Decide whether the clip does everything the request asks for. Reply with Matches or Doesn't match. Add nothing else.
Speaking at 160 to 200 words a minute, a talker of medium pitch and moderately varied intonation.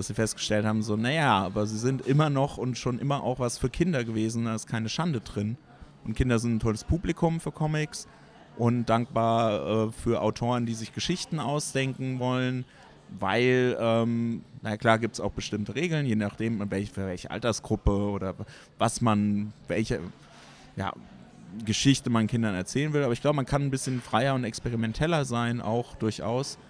Doesn't match